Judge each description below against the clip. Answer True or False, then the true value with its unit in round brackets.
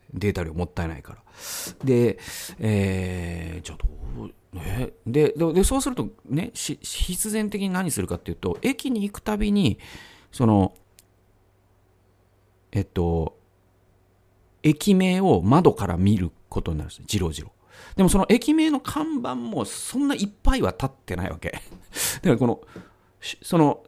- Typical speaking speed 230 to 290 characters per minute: True (275 characters per minute)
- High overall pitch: False (95 Hz)